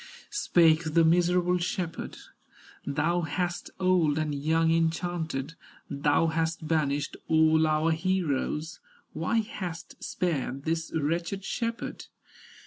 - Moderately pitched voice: Yes, medium, 165 Hz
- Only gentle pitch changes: Yes, narrow, 2.1 semitones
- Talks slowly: Yes, slow, 105 wpm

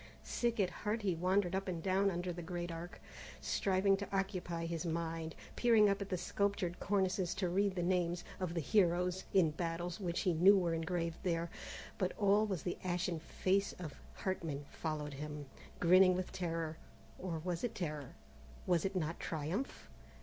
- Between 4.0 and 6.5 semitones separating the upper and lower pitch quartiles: No, narrow, 2.5 semitones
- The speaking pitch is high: No, medium, 180 Hz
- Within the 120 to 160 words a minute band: No, average, 170 wpm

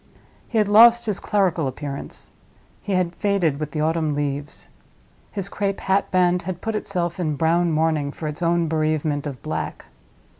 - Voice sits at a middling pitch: Yes, medium, 170 Hz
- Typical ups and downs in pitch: Yes, average, 4.2 semitones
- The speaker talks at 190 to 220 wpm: No, average, 160 wpm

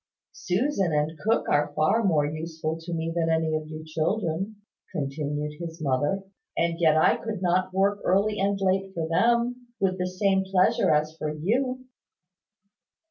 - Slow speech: No, average, 160 wpm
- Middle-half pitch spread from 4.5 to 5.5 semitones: No, average, 3.9 semitones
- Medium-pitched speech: Yes, medium, 170 Hz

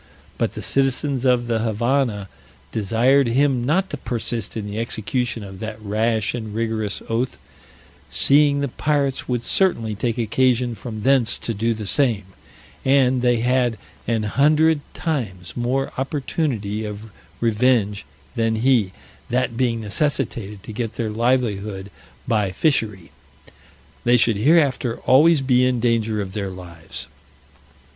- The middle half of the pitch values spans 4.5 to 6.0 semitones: No, average, 3.4 semitones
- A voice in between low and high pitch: No, low, 115 Hz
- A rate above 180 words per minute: No, slow, 135 wpm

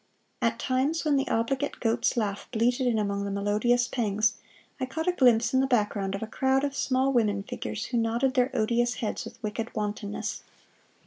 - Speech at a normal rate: Yes, average, 190 wpm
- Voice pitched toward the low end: No, high, 235 Hz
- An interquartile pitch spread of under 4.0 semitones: Yes, average, 3.6 semitones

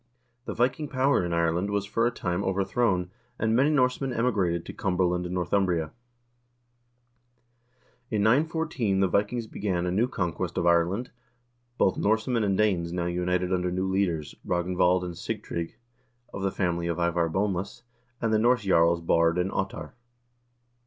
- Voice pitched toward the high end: No, very low, 95 Hz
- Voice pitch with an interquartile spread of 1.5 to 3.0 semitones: No, average, 4.1 semitones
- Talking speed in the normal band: Yes, average, 160 wpm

